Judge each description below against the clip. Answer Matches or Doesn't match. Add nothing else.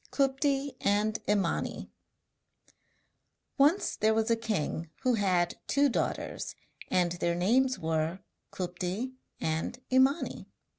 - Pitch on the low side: Doesn't match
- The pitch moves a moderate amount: Doesn't match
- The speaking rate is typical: Doesn't match